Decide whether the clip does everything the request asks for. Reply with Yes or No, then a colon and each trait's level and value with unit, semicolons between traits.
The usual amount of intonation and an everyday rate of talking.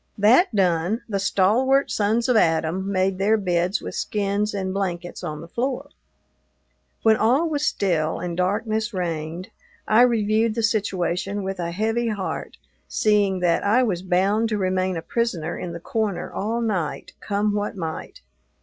Yes: average, 3.5 semitones; average, 160 wpm